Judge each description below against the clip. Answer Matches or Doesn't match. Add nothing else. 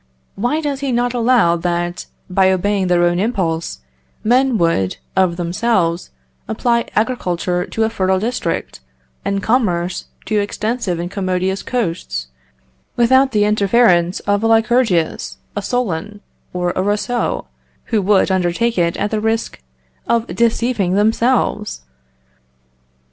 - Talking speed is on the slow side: Matches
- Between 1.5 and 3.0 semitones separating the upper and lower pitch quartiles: Doesn't match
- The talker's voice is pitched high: Matches